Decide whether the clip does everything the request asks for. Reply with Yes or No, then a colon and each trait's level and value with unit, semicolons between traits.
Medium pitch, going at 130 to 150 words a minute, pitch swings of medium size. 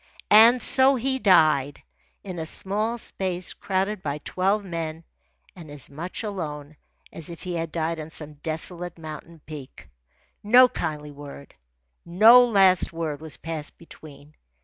Yes: medium, 170 Hz; average, 145 wpm; average, 4.3 semitones